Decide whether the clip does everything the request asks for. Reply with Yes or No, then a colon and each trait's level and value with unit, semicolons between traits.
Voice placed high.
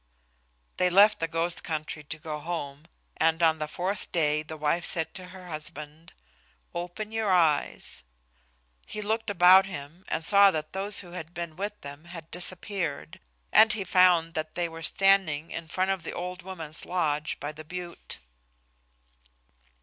No: medium, 170 Hz